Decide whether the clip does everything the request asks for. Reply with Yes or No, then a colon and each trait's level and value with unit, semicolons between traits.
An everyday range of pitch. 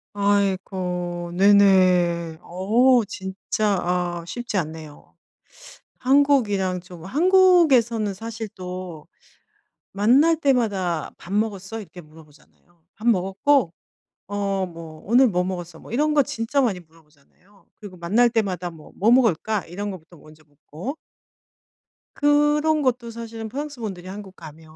Yes: average, 5.0 semitones